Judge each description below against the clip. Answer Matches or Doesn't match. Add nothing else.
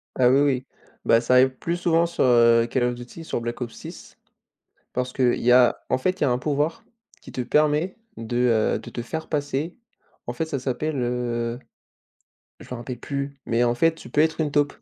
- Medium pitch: Doesn't match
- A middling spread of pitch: Matches